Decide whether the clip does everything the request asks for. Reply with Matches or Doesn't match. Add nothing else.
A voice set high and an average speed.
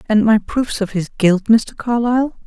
Matches